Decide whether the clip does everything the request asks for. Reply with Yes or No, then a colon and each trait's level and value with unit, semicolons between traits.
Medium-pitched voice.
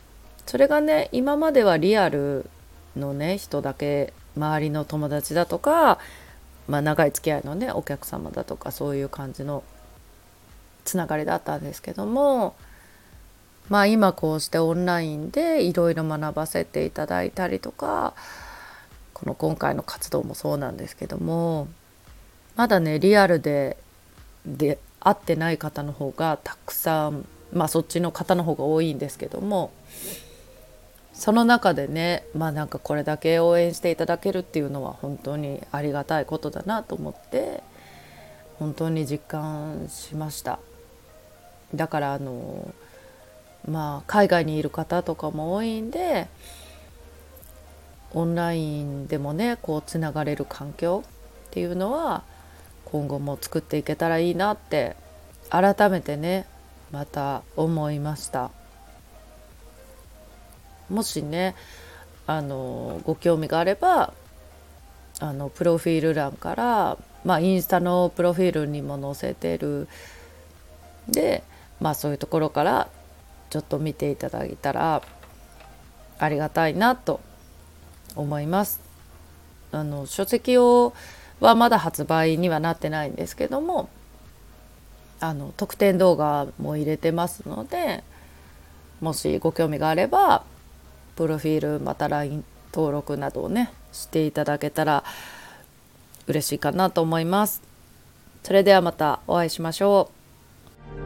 Yes: medium, 150 Hz